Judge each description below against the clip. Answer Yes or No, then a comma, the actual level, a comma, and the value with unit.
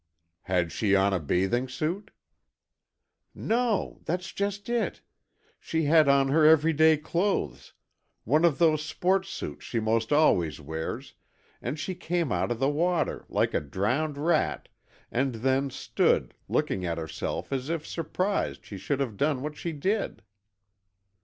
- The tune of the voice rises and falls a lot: Yes, wide, 6.7 semitones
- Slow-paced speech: No, average, 145 wpm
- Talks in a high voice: No, medium, 145 Hz